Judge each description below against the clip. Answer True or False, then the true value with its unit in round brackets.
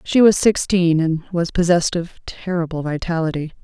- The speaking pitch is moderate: True (170 Hz)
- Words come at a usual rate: True (150 wpm)